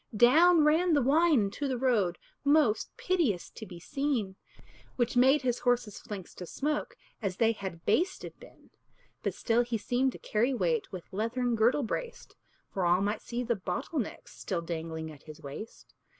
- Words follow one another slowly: No, average, 175 wpm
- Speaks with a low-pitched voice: No, high, 235 Hz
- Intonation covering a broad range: Yes, wide, 6.5 semitones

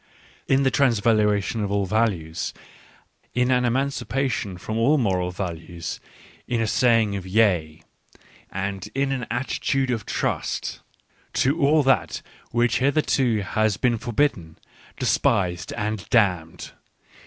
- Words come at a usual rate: No, slow, 130 wpm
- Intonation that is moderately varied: Yes, average, 4.7 semitones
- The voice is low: Yes, low, 110 Hz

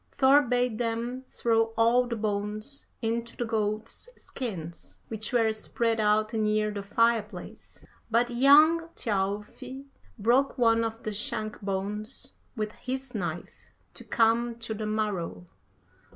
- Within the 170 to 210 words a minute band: No, slow, 135 wpm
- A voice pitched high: Yes, high, 225 Hz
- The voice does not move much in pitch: Yes, narrow, 2.3 semitones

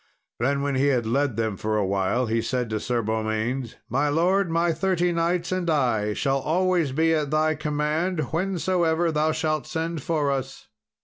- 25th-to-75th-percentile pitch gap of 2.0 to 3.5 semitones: No, average, 5.2 semitones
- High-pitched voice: No, medium, 150 Hz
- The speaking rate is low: No, average, 180 wpm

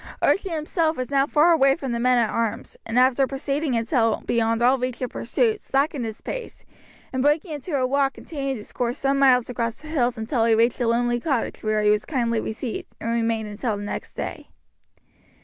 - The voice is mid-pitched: No, very high, 250 Hz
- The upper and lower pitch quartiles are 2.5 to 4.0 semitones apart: Yes, average, 3.2 semitones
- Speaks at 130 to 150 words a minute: No, average, 200 wpm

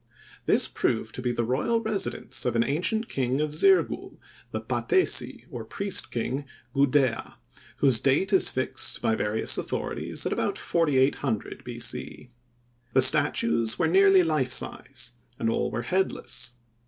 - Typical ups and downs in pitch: No, wide, 5.7 semitones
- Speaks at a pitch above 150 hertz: No, low, 135 Hz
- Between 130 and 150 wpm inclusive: Yes, average, 145 wpm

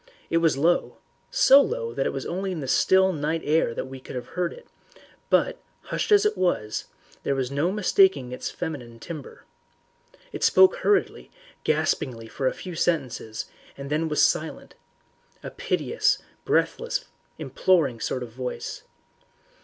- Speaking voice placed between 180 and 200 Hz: No, medium, 155 Hz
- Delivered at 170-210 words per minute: No, average, 155 wpm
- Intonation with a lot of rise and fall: Yes, wide, 6.4 semitones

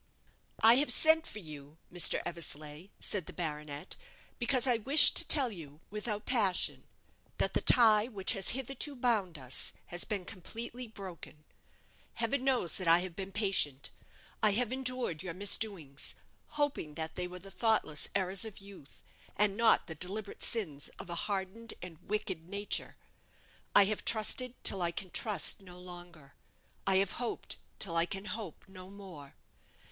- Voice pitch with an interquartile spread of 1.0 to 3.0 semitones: No, average, 4.8 semitones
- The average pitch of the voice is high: Yes, high, 195 Hz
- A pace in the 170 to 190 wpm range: No, average, 160 wpm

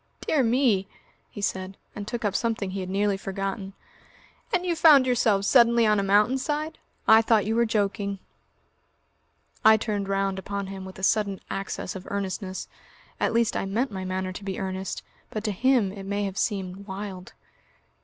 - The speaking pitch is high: Yes, high, 200 Hz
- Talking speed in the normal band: Yes, average, 180 wpm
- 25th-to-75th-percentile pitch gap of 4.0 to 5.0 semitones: No, average, 2.8 semitones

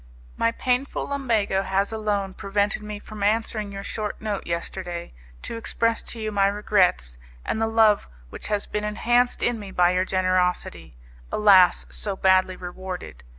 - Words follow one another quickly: No, average, 155 wpm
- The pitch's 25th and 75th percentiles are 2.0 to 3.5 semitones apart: Yes, narrow, 2.6 semitones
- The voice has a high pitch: Yes, high, 205 Hz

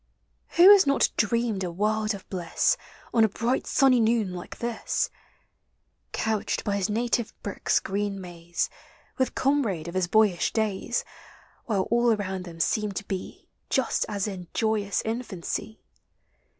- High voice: Yes, high, 210 Hz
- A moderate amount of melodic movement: Yes, average, 3.5 semitones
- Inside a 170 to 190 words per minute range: No, average, 145 wpm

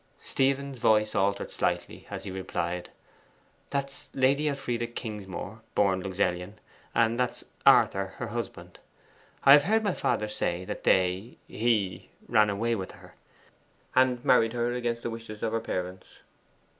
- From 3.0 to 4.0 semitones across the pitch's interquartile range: No, average, 4.4 semitones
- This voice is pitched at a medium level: No, low, 115 Hz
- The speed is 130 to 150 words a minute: Yes, average, 145 wpm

